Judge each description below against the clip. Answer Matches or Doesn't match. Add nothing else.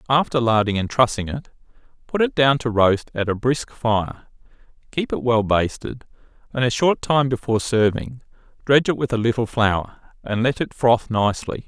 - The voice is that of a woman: Doesn't match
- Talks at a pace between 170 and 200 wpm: Matches